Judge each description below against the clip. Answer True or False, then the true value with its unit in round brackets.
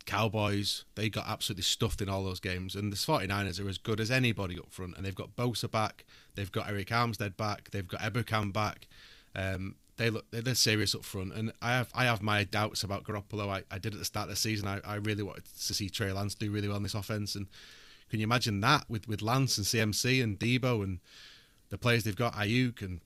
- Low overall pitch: True (105 Hz)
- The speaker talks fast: True (235 wpm)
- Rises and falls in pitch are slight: True (2.3 semitones)